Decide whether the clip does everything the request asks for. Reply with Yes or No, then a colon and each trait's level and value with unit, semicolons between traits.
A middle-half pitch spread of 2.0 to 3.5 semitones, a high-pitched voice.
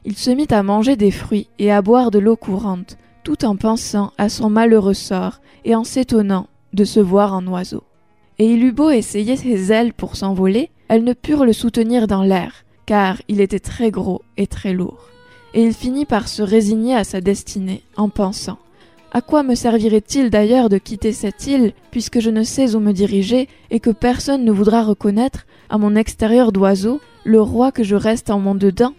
Yes: average, 2.8 semitones; high, 220 Hz